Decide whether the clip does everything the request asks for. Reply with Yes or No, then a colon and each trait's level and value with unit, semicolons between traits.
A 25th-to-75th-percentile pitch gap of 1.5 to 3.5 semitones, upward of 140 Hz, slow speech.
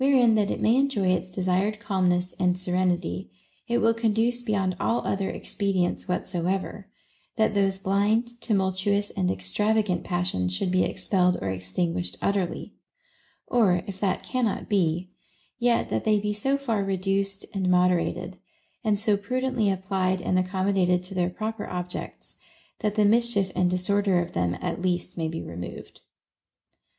No: average, 2.8 semitones; high, 190 Hz; average, 155 wpm